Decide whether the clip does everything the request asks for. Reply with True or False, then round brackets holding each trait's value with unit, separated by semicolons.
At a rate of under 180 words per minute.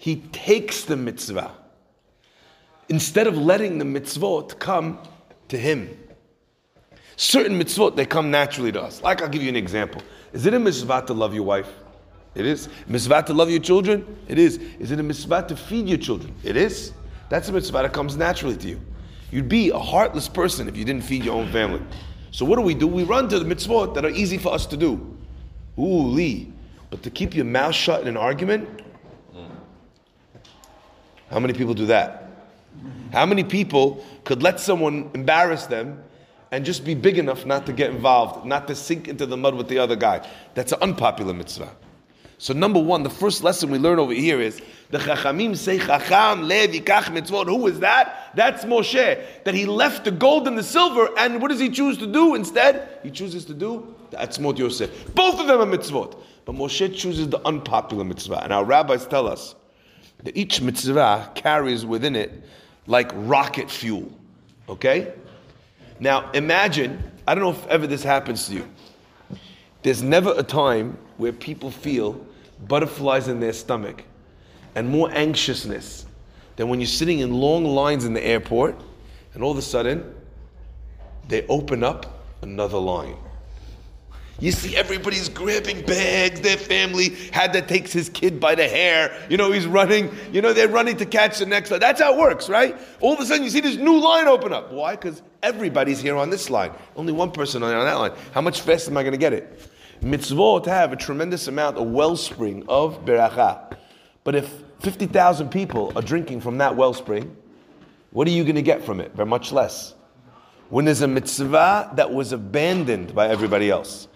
False (190 wpm)